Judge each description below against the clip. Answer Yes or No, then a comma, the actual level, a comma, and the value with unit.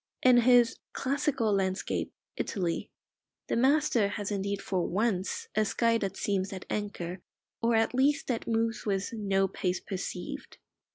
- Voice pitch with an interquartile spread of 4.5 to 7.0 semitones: No, average, 3.6 semitones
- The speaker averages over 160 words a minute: No, average, 145 wpm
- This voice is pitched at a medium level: No, high, 210 Hz